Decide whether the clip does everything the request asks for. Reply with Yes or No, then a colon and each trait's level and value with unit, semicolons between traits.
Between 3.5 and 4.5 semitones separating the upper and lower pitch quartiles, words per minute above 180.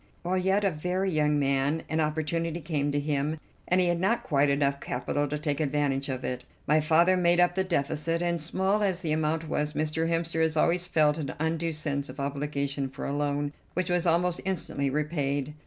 No: average, 3.1 semitones; fast, 205 wpm